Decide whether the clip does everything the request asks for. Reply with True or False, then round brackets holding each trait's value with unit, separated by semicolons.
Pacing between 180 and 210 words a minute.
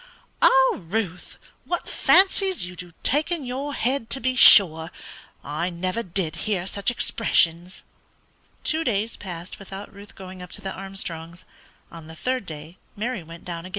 False (160 wpm)